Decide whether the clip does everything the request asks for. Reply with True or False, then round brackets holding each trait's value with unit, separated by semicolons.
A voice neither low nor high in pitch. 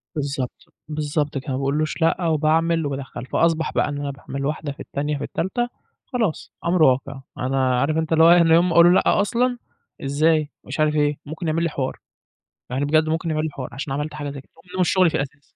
True (155 Hz)